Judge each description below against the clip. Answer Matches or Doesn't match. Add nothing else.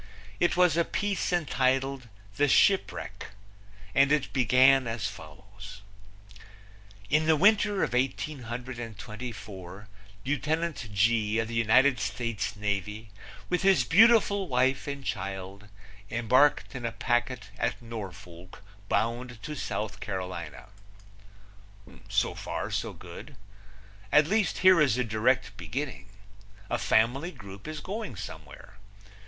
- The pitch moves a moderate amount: Doesn't match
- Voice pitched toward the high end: Doesn't match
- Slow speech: Matches